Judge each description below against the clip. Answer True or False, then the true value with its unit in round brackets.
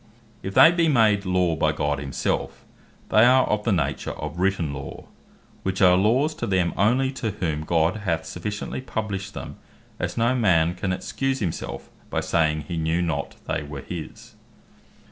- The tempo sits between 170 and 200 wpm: True (175 wpm)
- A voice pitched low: True (95 Hz)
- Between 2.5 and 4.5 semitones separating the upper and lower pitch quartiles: False (5.2 semitones)